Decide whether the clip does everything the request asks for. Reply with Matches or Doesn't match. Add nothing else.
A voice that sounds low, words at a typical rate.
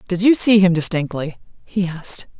Doesn't match